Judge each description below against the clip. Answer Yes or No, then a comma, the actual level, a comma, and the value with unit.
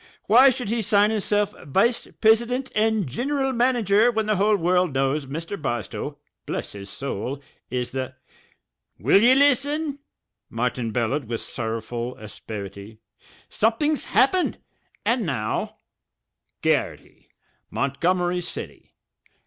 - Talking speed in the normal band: No, slow, 115 wpm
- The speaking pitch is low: No, high, 190 Hz